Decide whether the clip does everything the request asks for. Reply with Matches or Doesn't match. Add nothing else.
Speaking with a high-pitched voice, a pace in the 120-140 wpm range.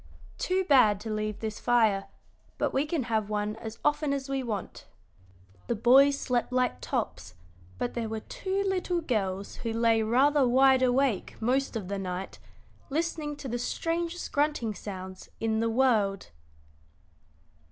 Doesn't match